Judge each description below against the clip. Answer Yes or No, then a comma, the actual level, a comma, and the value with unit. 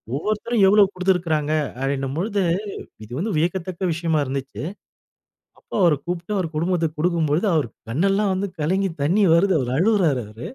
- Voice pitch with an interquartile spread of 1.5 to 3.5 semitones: No, average, 4.3 semitones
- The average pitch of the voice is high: No, medium, 170 Hz